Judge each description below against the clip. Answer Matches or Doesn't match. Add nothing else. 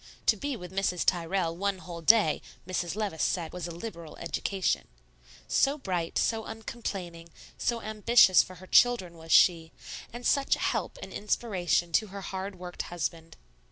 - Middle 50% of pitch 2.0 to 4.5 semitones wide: Matches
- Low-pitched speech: Doesn't match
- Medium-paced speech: Matches